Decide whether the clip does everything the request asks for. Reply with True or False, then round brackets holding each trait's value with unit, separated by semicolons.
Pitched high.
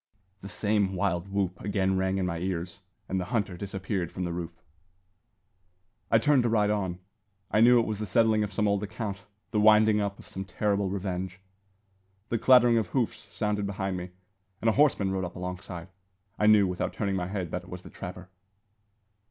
False (100 Hz)